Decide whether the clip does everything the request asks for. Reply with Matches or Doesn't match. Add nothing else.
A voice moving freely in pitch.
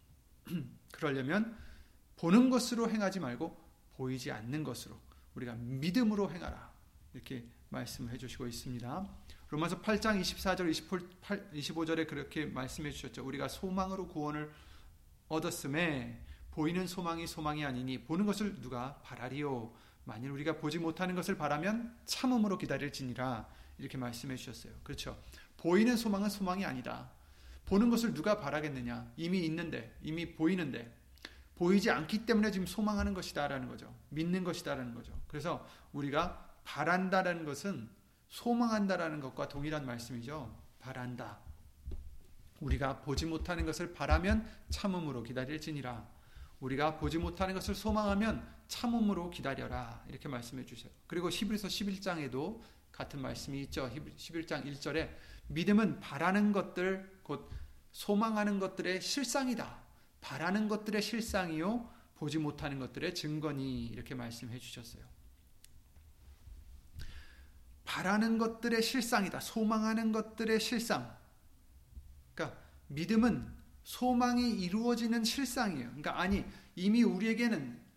Matches